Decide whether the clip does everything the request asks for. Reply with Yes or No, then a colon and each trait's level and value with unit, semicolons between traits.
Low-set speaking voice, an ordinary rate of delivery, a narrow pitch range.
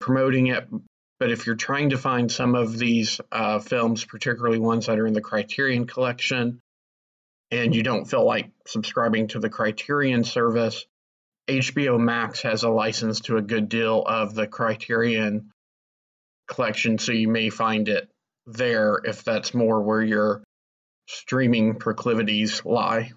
Yes: low, 115 Hz; average, 150 wpm; narrow, 1.7 semitones